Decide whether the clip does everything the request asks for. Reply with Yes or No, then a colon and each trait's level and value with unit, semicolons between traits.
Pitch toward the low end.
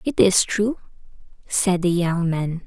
No: medium, 185 Hz